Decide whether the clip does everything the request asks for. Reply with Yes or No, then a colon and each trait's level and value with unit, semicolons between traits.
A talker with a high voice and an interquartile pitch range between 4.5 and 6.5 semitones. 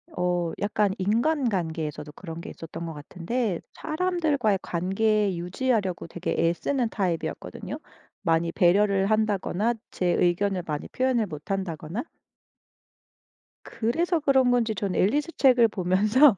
Yes: high, 200 Hz; wide, 5.4 semitones